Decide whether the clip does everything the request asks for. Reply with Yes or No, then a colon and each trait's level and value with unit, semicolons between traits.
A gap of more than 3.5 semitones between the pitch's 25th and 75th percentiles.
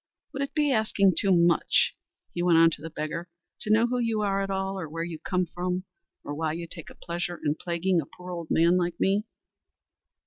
No: average, 2.9 semitones